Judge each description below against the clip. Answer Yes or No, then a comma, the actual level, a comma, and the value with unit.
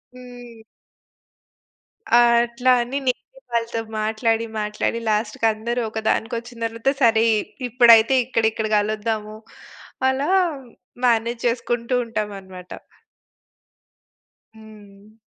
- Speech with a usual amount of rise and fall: No, narrow, 1.8 semitones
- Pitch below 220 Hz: No, high, 230 Hz